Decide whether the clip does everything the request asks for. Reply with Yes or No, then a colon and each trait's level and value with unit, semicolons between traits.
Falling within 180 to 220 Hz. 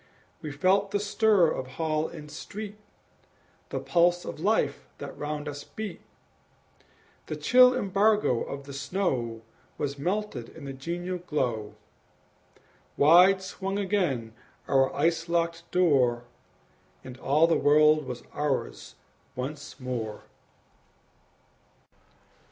No: medium, 155 Hz